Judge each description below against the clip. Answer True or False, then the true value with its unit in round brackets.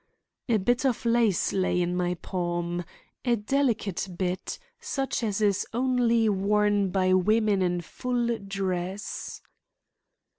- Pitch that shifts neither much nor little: True (4.2 semitones)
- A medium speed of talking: False (120 wpm)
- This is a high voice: True (205 Hz)